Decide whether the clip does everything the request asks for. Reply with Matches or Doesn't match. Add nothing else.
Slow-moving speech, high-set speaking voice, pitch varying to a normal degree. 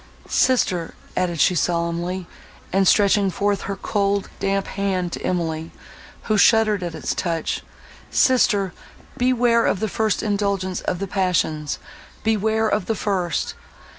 Matches